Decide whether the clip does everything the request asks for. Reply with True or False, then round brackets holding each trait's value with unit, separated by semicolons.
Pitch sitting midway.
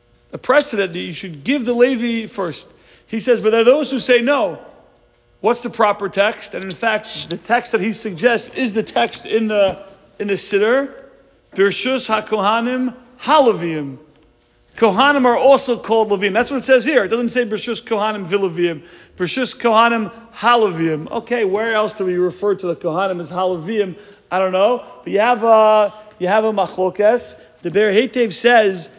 False (215 Hz)